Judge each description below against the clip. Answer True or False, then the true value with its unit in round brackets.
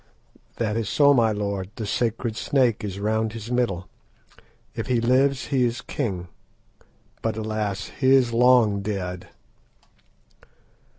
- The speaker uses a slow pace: True (130 wpm)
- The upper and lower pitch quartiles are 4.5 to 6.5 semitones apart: False (3.2 semitones)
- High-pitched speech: False (110 Hz)